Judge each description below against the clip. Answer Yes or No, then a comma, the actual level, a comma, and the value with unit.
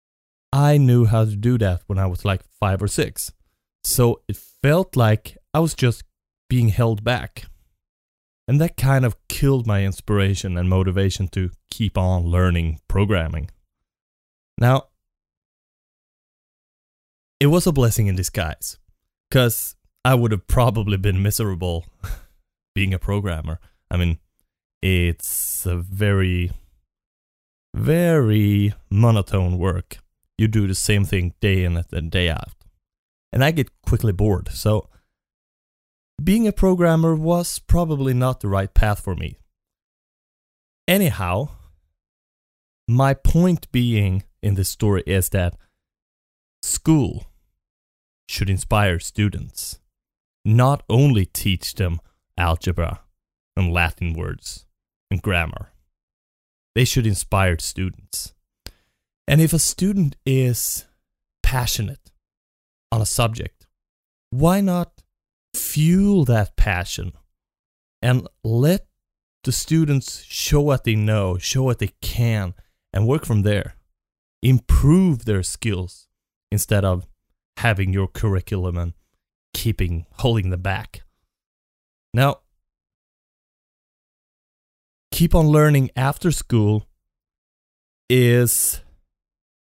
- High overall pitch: No, low, 100 Hz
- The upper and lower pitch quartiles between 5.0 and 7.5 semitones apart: Yes, wide, 5.6 semitones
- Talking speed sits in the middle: No, slow, 110 wpm